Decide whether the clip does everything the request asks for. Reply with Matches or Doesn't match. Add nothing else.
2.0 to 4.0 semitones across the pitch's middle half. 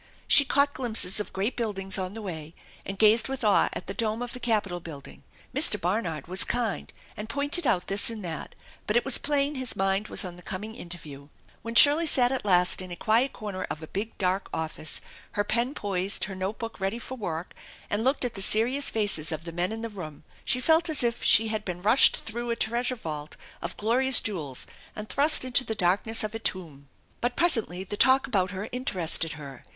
Doesn't match